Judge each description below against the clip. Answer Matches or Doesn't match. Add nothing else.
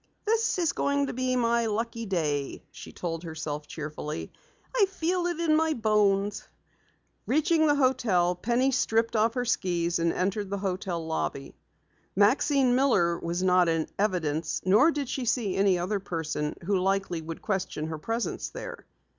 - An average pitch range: Doesn't match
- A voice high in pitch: Matches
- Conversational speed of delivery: Matches